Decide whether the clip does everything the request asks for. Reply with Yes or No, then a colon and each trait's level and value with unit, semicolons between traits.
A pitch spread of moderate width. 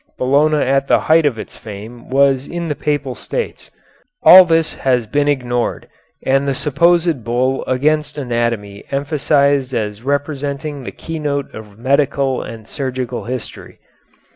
Yes: average, 3.1 semitones